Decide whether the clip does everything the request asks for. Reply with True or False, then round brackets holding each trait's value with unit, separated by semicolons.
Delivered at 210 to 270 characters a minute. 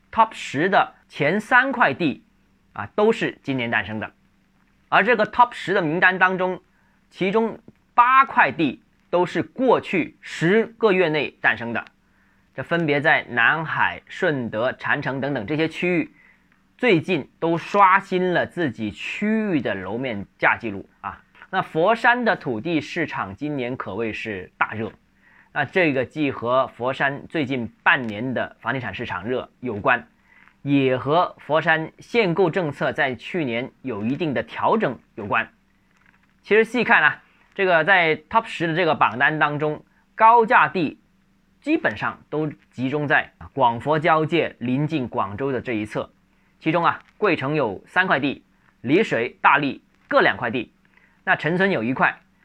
True (225 characters per minute)